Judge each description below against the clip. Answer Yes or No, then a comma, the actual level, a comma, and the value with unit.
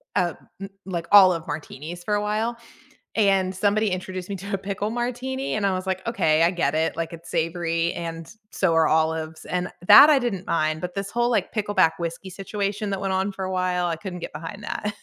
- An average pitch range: Yes, average, 3.5 semitones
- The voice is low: No, medium, 185 Hz